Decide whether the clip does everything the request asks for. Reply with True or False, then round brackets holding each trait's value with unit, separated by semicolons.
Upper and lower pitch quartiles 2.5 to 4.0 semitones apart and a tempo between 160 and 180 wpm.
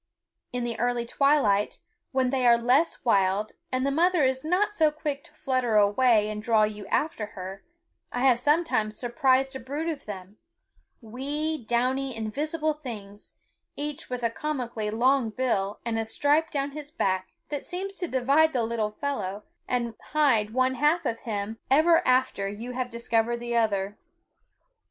False (4.7 semitones; 165 wpm)